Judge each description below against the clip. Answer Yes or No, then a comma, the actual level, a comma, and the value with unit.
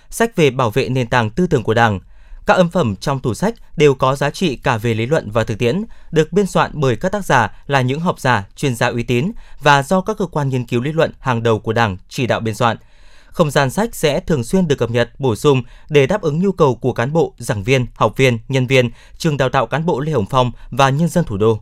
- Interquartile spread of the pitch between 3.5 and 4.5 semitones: No, average, 5.1 semitones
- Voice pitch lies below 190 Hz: Yes, low, 135 Hz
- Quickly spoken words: Yes, fast, 270 wpm